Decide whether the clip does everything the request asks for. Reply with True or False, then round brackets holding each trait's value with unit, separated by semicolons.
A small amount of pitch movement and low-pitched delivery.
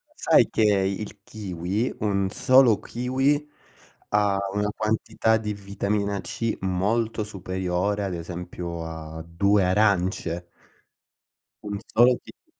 False (3.0 semitones; 100 Hz)